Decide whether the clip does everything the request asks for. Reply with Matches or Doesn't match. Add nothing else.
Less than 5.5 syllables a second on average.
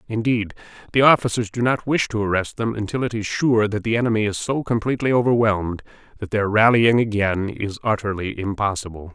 Doesn't match